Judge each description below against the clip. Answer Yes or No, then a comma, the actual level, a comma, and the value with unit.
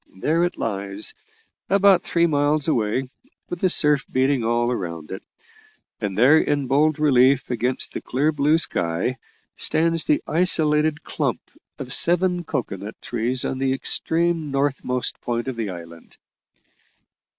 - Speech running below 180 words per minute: Yes, average, 140 wpm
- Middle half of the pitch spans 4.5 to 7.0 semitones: Yes, average, 5.0 semitones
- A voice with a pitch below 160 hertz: Yes, low, 135 Hz